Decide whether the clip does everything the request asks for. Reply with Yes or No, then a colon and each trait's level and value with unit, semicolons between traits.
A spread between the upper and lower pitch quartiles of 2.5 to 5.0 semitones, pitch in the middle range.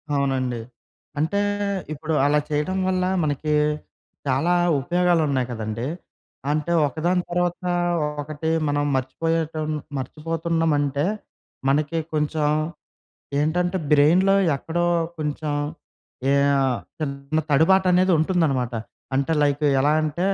Yes: average, 3.3 semitones; medium, 155 Hz